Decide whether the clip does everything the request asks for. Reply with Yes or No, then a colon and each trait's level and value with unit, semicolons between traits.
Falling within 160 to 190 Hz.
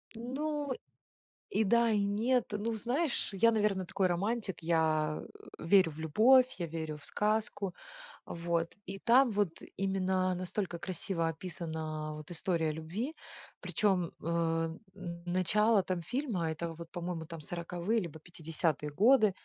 Yes: medium, 185 Hz